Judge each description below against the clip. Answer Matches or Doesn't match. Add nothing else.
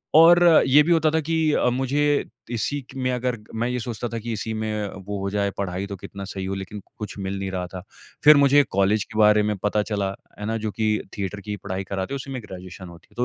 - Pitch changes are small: Doesn't match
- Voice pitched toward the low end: Matches